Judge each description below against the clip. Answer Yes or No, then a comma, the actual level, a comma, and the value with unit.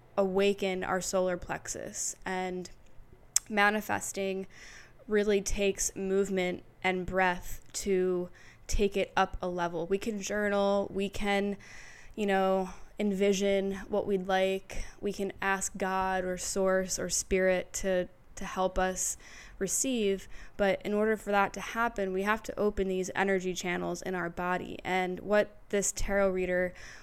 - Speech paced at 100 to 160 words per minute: Yes, average, 140 wpm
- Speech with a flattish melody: Yes, narrow, 1.4 semitones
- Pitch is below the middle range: No, high, 195 Hz